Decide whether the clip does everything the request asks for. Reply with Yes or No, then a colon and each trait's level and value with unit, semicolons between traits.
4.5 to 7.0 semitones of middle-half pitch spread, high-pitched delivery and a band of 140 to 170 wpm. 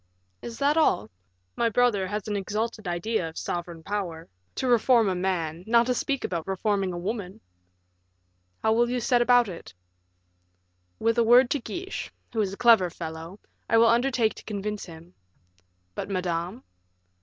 Yes: average, 4.9 semitones; high, 210 Hz; average, 165 wpm